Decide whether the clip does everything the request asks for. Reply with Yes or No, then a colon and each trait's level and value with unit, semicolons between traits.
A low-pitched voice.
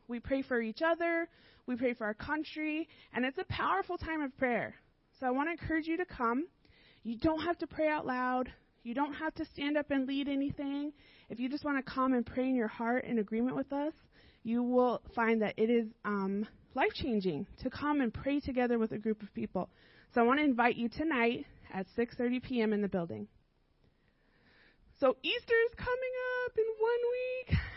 No: very high, 260 Hz